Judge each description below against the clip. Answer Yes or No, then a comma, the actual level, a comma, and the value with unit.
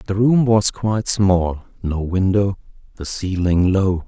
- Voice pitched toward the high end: No, very low, 95 Hz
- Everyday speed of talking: Yes, average, 145 wpm